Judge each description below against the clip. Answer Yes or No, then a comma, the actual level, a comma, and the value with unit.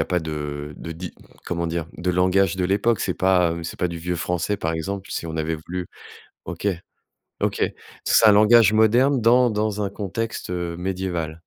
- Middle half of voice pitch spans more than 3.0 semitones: Yes, average, 3.7 semitones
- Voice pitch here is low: Yes, very low, 90 Hz